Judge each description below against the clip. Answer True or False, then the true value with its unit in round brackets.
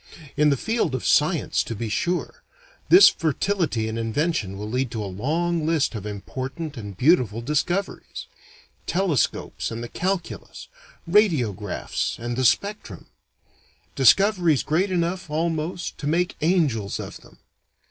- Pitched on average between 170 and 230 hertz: False (150 Hz)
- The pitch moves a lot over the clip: True (7.1 semitones)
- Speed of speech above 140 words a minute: False (135 wpm)